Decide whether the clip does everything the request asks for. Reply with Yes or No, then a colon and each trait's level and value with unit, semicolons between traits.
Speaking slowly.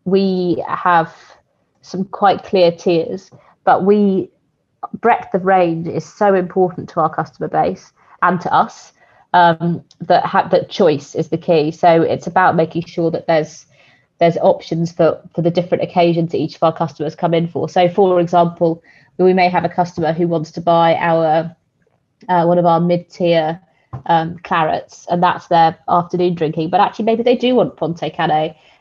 No: average, 175 wpm